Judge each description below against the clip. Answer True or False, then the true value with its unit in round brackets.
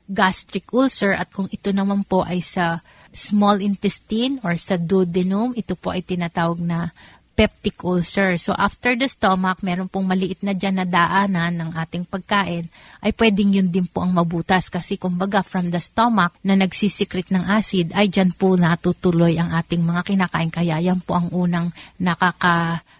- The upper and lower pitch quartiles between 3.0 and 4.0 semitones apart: False (2.4 semitones)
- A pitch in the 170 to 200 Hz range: True (185 Hz)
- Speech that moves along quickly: True (170 wpm)